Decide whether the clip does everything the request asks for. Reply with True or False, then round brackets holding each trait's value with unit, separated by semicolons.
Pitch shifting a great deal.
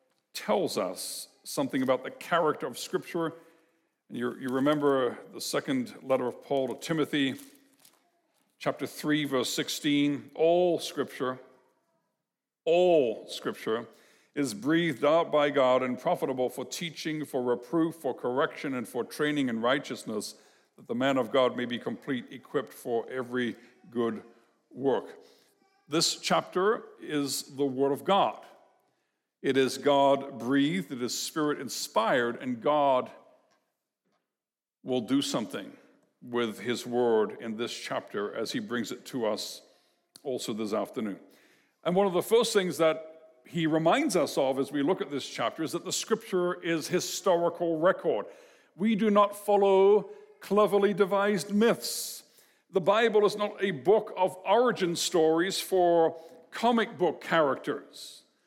True (6.4 semitones)